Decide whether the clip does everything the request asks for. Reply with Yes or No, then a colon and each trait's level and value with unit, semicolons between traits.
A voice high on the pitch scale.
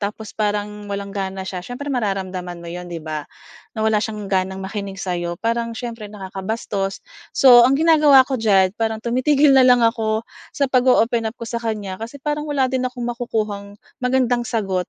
Yes: high, 220 Hz